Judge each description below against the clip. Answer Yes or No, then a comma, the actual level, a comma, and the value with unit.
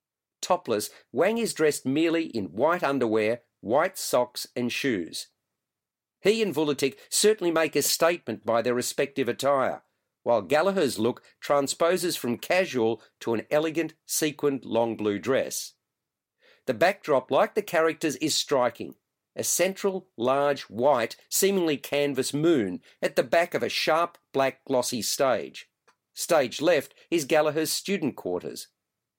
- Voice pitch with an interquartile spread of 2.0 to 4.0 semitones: No, average, 5.1 semitones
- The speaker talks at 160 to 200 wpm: No, slow, 135 wpm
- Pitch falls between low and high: Yes, medium, 150 Hz